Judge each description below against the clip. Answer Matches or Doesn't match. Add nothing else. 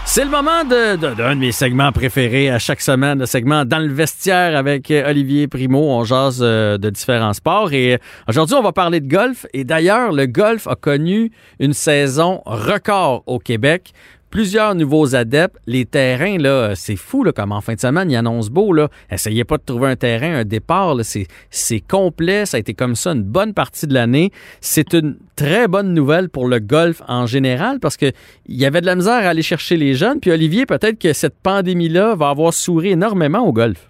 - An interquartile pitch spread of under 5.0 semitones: Doesn't match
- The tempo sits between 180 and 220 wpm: Matches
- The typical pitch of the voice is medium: Matches